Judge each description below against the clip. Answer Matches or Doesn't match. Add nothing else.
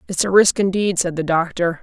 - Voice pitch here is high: Doesn't match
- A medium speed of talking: Doesn't match